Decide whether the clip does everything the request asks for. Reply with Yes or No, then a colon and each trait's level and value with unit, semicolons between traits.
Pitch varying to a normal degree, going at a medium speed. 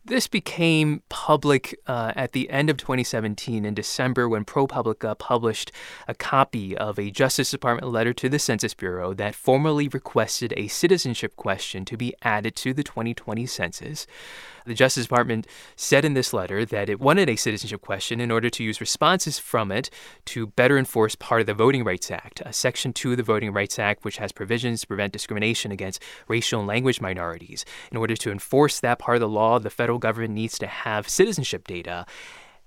Yes: average, 3.5 semitones; average, 190 wpm